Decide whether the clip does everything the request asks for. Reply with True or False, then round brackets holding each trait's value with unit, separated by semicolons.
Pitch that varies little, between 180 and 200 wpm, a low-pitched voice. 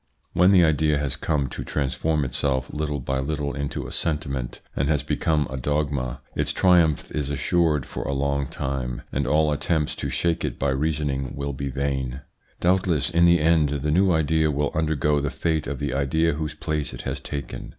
True (2.3 semitones; 190 wpm; 75 Hz)